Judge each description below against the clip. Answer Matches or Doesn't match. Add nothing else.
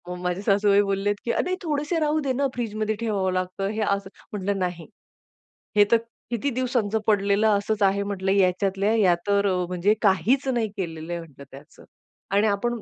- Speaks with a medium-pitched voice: Doesn't match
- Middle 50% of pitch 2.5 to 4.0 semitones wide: Matches